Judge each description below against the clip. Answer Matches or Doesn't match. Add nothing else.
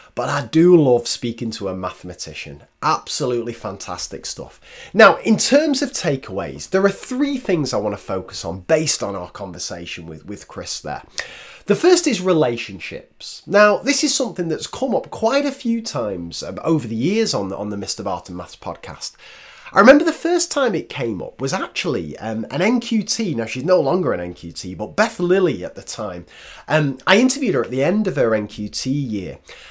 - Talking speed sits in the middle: Matches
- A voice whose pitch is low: Doesn't match